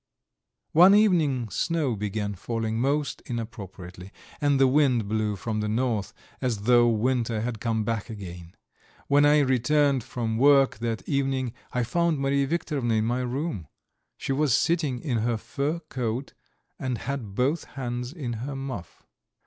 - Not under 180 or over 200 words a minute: No, average, 150 wpm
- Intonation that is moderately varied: Yes, average, 4.0 semitones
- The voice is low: Yes, low, 125 Hz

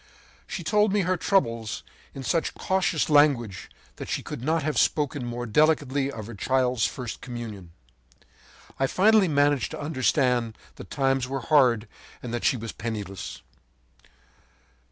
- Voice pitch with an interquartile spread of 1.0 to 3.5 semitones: No, average, 4.6 semitones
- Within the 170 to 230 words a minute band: No, average, 145 wpm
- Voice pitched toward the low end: Yes, low, 130 Hz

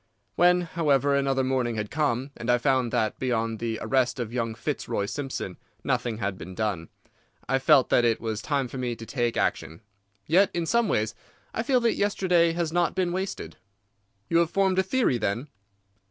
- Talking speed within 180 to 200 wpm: Yes, average, 185 wpm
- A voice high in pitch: No, low, 130 Hz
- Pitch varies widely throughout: Yes, wide, 6.8 semitones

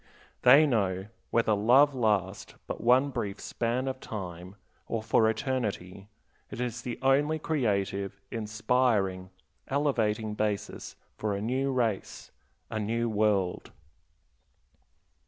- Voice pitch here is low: Yes, low, 110 Hz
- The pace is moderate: No, slow, 115 wpm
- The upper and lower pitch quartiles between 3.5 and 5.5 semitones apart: Yes, average, 3.9 semitones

